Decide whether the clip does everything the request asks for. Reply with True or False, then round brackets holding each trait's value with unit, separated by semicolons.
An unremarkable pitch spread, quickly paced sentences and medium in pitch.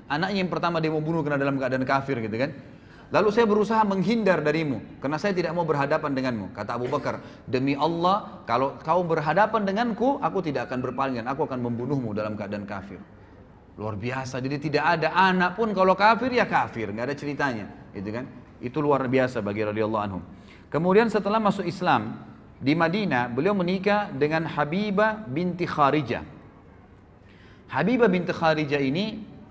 False (7.4 semitones; 160 wpm; 145 Hz)